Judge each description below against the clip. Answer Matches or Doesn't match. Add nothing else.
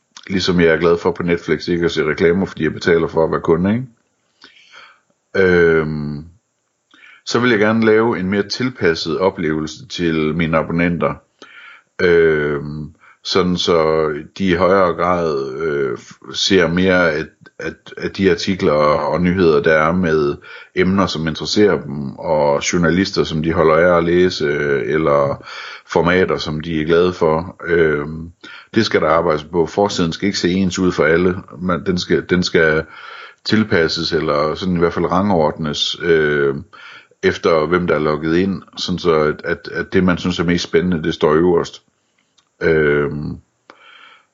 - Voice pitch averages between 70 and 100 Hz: Matches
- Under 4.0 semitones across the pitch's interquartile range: Matches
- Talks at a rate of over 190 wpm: Doesn't match